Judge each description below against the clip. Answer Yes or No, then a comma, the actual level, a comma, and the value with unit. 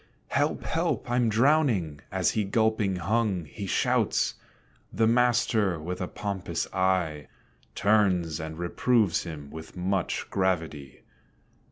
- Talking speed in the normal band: No, slow, 120 wpm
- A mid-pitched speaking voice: No, very low, 95 Hz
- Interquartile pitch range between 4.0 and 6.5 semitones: Yes, average, 4.8 semitones